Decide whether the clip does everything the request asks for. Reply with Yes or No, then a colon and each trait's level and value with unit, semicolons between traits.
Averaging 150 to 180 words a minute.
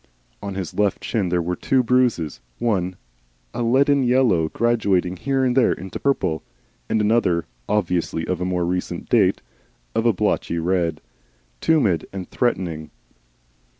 No: average, 140 wpm